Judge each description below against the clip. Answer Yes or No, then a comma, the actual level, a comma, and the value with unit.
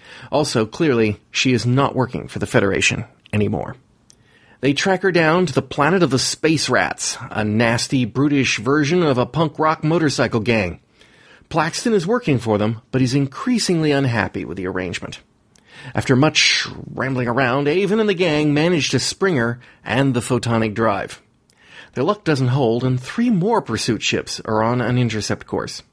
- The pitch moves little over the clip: No, average, 5.1 semitones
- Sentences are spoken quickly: No, average, 170 wpm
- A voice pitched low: Yes, low, 130 Hz